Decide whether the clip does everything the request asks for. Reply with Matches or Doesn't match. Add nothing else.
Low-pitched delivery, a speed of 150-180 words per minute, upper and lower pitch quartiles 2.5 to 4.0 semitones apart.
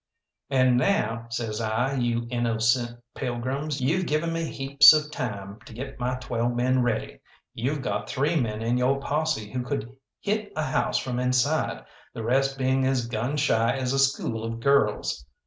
Matches